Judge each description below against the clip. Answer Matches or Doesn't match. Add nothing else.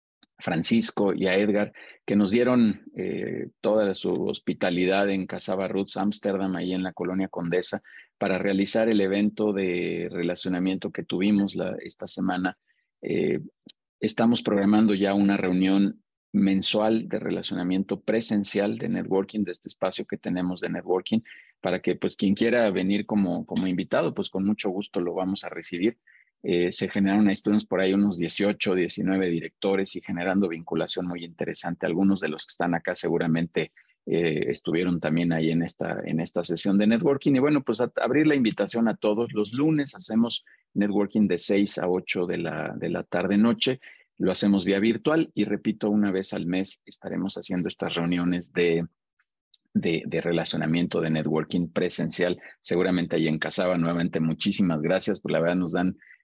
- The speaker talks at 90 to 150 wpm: Doesn't match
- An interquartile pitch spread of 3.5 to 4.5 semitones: Doesn't match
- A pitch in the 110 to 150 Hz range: Doesn't match